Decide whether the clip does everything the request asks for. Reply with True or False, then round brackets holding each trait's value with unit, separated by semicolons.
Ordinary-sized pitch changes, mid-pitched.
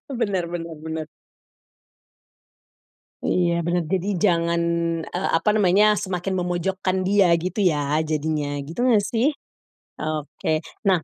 True (3.3 semitones; 175 Hz)